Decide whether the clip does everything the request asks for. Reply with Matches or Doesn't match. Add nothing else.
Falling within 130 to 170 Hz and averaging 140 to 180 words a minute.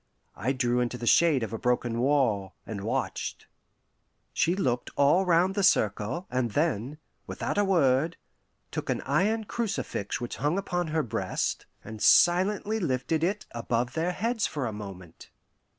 Matches